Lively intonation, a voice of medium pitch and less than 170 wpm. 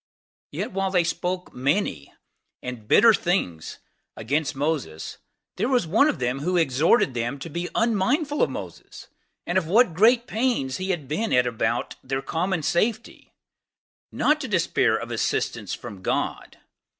Yes: wide, 8.4 semitones; medium, 175 Hz; average, 150 wpm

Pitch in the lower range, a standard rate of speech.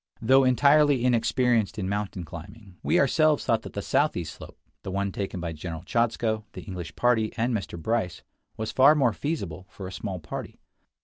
Yes: low, 110 Hz; average, 180 wpm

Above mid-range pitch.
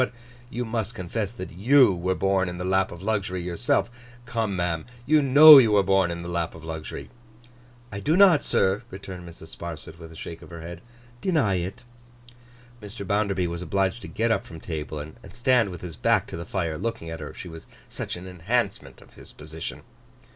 No: very low, 95 Hz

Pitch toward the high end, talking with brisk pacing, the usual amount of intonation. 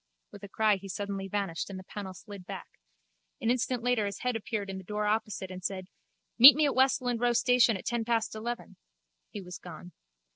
Yes: high, 210 Hz; fast, 210 wpm; average, 3.6 semitones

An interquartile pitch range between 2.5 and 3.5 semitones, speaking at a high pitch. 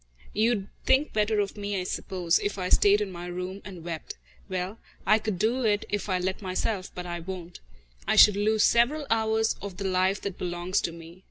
Yes: average, 2.8 semitones; high, 195 Hz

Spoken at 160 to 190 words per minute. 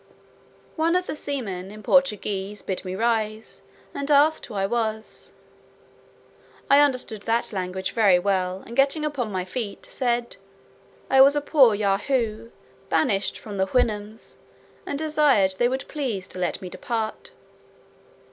No: average, 145 wpm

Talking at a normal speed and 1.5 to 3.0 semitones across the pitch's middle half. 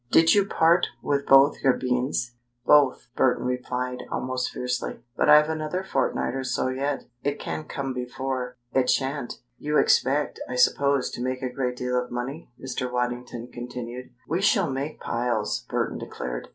Yes: average, 165 wpm; narrow, 2.4 semitones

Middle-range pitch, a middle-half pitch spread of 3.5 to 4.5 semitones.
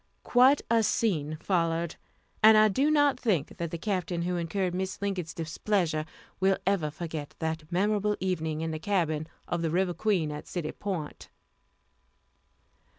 Yes: medium, 175 Hz; average, 4.1 semitones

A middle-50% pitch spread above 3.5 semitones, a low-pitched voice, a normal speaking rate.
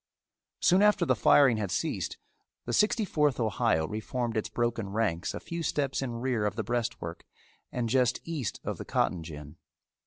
Yes: average, 4.7 semitones; low, 120 Hz; average, 175 wpm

